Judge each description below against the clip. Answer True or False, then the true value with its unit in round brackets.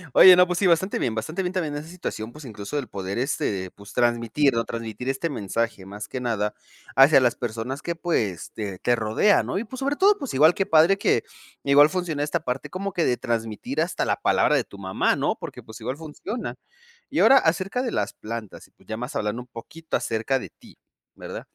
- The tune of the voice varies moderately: False (7.3 semitones)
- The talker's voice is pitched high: False (135 Hz)